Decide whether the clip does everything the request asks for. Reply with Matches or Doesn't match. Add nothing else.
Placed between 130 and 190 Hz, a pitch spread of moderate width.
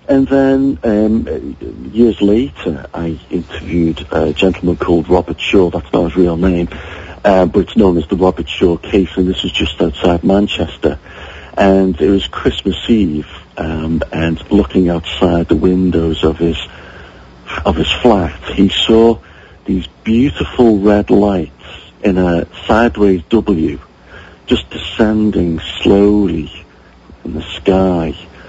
Doesn't match